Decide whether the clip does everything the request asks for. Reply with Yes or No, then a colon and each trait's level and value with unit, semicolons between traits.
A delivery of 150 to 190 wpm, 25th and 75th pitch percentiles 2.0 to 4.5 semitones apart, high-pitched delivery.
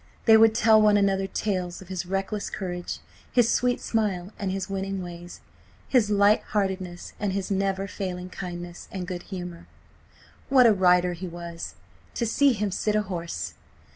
Yes: average, 170 wpm; average, 2.8 semitones; high, 195 Hz